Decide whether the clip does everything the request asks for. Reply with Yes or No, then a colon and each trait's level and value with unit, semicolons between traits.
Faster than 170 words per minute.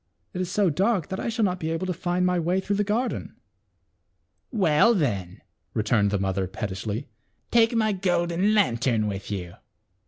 Yes: average, 180 wpm